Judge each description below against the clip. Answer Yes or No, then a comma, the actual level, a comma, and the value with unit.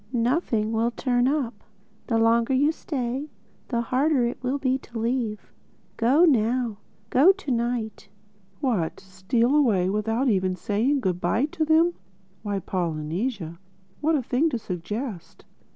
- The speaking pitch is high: Yes, high, 235 Hz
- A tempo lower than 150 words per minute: Yes, slow, 135 wpm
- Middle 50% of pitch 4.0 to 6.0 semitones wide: Yes, average, 4.3 semitones